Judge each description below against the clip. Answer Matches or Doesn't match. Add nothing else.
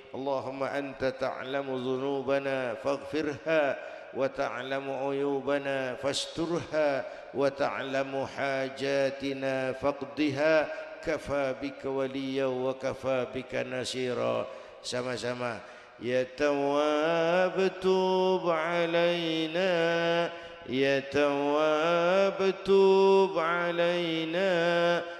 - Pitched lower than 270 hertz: Matches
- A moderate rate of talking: Doesn't match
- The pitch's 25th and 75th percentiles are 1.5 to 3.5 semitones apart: Doesn't match